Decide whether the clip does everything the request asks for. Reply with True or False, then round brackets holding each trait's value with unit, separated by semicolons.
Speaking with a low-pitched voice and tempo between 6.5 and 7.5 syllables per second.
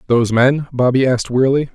True (130 Hz; 6.6 syllables/s)